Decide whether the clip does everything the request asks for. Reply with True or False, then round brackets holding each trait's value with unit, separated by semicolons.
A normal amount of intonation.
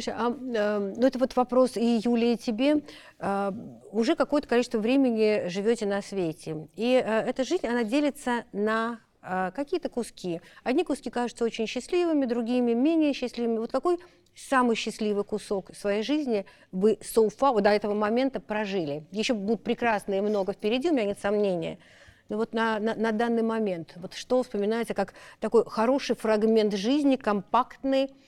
True (3.4 semitones)